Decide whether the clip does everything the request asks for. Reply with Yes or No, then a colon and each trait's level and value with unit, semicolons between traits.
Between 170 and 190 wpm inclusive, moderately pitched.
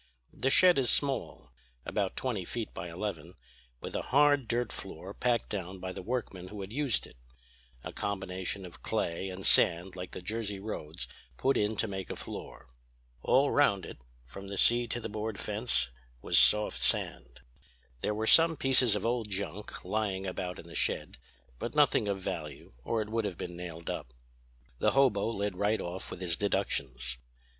No: average, 180 wpm; low, 100 Hz